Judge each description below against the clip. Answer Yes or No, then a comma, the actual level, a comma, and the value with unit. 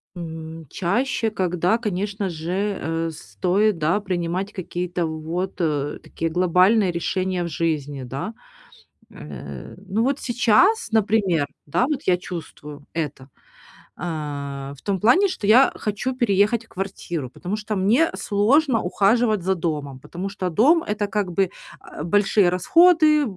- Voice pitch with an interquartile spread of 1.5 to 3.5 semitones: No, average, 4.7 semitones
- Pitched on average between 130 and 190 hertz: Yes, medium, 185 Hz